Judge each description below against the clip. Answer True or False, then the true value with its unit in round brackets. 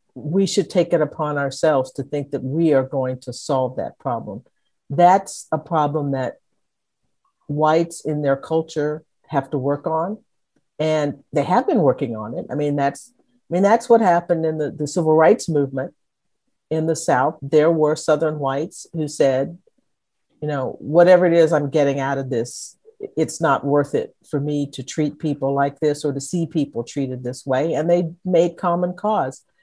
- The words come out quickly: False (185 wpm)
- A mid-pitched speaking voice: True (155 Hz)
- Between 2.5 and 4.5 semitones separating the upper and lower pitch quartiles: True (3.5 semitones)